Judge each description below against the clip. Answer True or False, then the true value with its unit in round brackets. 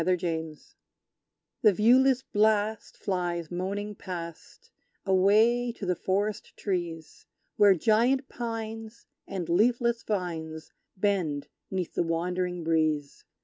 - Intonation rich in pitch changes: False (4.3 semitones)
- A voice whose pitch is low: False (190 Hz)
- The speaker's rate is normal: False (110 wpm)